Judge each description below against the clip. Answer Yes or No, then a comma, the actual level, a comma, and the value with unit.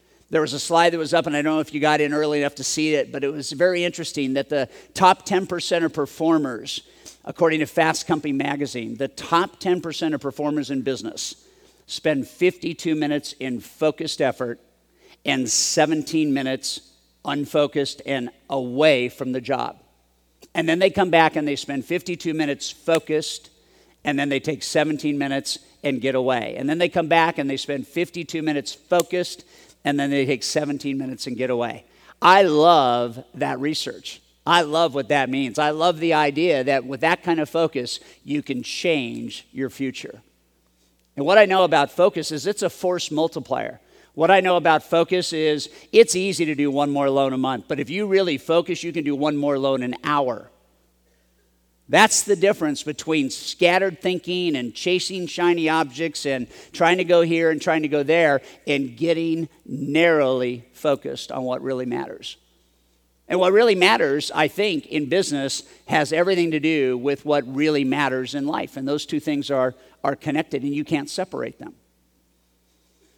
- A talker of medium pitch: Yes, medium, 150 Hz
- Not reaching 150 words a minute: No, average, 180 wpm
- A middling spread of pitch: Yes, average, 3.5 semitones